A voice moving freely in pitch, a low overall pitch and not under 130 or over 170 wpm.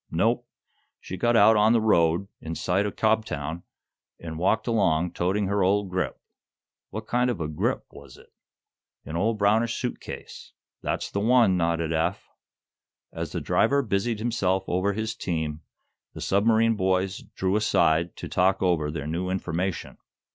No: average, 4.3 semitones; very low, 95 Hz; average, 160 wpm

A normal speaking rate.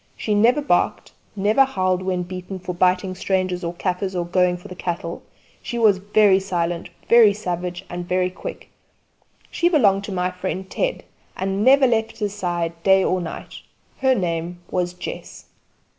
Yes: average, 165 wpm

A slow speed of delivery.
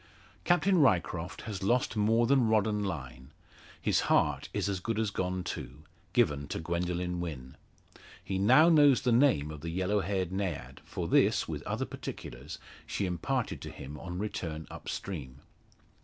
No: average, 165 wpm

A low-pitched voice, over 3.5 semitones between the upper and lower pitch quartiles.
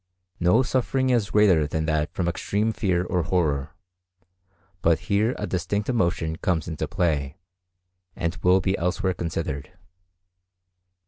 Yes: very low, 90 Hz; average, 4.0 semitones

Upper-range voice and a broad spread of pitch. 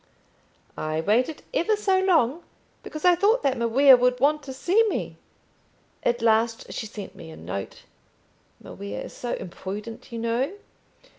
Yes: high, 245 Hz; wide, 6.0 semitones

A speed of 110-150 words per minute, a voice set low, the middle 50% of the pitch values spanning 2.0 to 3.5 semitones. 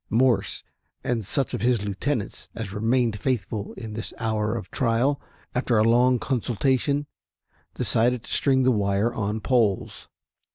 Yes: average, 140 wpm; low, 115 Hz; average, 2.9 semitones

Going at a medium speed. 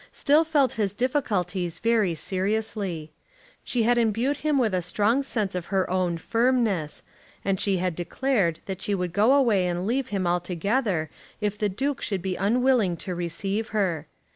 Yes: average, 165 wpm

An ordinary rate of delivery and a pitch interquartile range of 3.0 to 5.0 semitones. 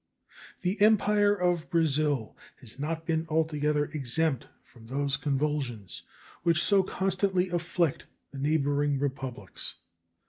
No: slow, 110 wpm; average, 3.9 semitones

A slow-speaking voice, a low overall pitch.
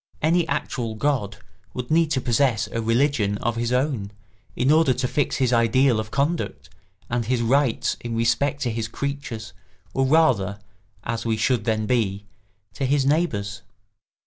No: average, 160 wpm; low, 120 Hz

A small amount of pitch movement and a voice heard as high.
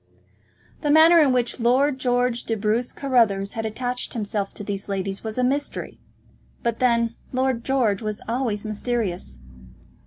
No: average, 3.2 semitones; high, 235 Hz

